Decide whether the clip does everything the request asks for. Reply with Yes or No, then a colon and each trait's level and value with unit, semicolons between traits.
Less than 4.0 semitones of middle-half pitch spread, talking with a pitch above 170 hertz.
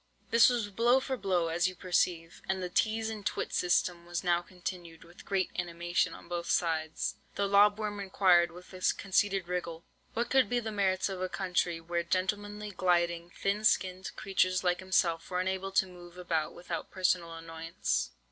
Yes: narrow, 2.4 semitones; medium, 185 Hz